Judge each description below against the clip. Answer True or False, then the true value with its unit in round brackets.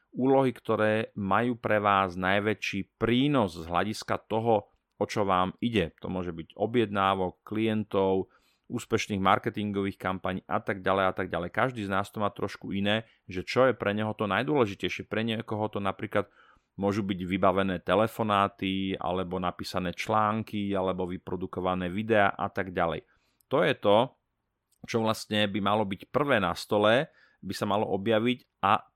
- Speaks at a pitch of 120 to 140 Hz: False (100 Hz)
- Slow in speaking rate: False (155 wpm)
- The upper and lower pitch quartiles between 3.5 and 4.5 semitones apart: False (2.5 semitones)